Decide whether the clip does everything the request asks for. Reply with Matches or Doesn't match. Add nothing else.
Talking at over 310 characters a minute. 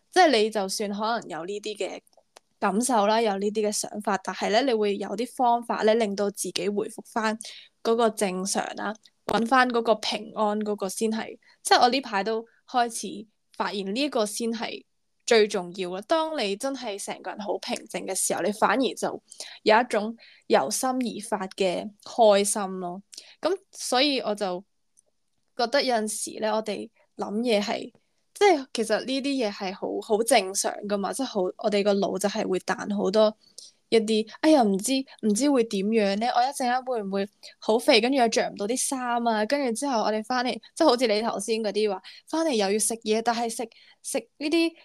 Doesn't match